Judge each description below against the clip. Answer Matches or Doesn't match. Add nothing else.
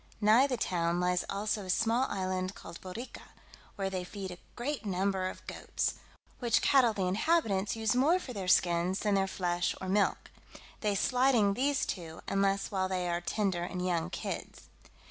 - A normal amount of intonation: Matches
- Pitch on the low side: Doesn't match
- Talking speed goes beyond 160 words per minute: Matches